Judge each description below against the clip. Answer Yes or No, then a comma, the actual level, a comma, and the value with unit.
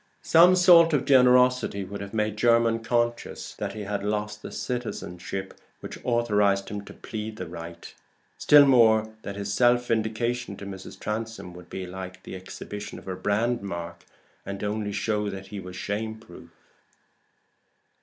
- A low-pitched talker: Yes, low, 105 Hz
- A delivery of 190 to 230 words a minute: No, average, 160 wpm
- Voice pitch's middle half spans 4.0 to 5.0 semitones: No, average, 3.2 semitones